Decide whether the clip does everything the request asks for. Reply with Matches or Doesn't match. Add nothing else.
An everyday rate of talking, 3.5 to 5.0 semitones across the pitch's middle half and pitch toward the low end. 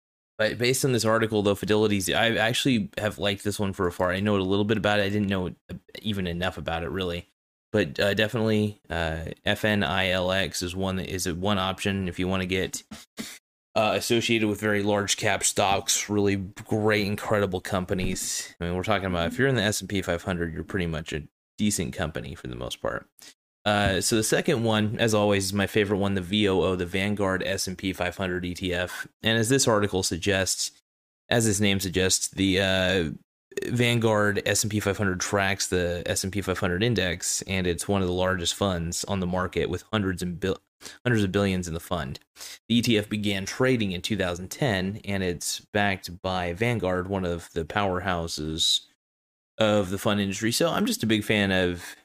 Doesn't match